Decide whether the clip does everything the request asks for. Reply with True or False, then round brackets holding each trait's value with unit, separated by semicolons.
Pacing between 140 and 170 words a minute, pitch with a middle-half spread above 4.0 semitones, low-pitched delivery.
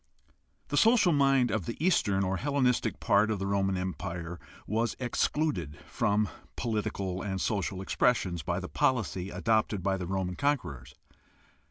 True (150 wpm; 4.7 semitones; 100 Hz)